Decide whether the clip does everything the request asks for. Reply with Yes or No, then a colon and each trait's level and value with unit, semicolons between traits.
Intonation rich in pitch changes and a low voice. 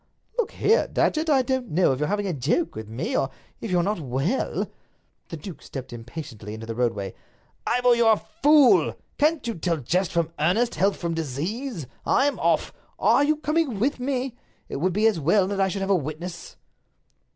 No: wide, 8.7 semitones; high, 190 Hz